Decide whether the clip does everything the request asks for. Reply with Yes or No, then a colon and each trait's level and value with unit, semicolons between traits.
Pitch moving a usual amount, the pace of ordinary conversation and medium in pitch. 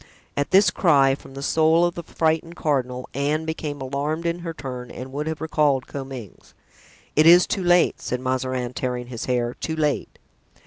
Yes: average, 3.8 semitones; average, 180 wpm; medium, 145 Hz